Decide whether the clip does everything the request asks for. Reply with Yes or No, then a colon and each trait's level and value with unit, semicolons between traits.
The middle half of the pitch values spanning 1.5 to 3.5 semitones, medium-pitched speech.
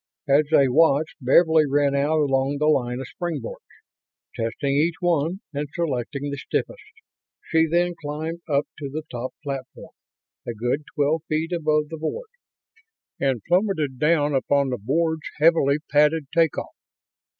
Yes: average, 2.8 semitones; medium, 150 Hz